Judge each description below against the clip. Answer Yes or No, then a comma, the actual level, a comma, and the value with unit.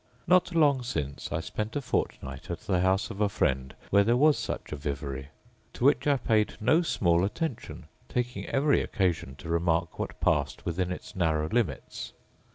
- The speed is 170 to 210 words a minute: Yes, average, 175 wpm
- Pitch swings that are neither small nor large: No, wide, 7.5 semitones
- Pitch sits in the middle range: No, very low, 95 Hz